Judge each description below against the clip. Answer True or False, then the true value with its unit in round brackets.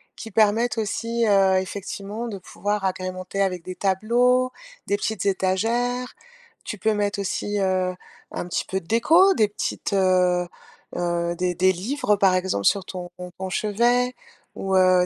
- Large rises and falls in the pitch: False (3.3 semitones)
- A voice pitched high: True (195 Hz)